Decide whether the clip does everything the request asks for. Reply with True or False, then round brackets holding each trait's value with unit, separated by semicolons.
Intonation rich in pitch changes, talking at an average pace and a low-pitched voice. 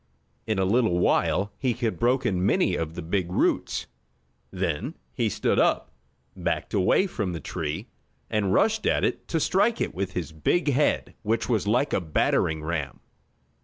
True (5.9 semitones; 165 wpm; 100 Hz)